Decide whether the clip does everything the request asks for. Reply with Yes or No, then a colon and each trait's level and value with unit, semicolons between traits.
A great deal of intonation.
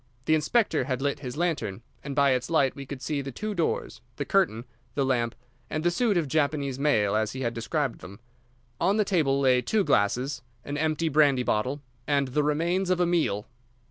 No: average, 3.9 semitones